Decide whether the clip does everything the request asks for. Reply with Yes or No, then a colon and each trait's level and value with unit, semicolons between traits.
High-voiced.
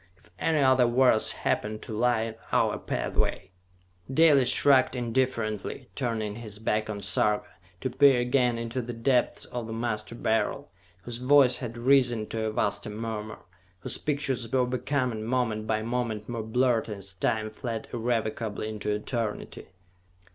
No: low, 115 Hz